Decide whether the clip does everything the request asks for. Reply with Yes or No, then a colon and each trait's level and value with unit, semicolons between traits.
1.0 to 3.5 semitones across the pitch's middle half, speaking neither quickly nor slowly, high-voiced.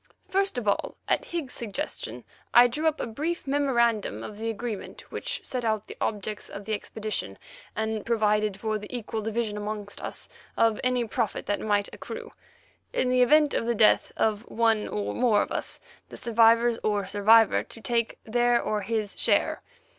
Yes: narrow, 2.4 semitones; average, 175 wpm; high, 225 Hz